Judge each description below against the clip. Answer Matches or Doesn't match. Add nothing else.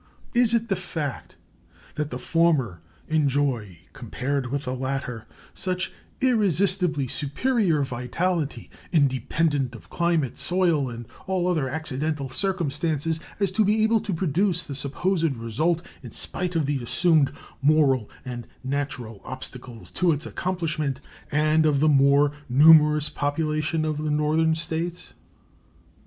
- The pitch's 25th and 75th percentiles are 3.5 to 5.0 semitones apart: Matches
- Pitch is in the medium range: Matches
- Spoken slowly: Matches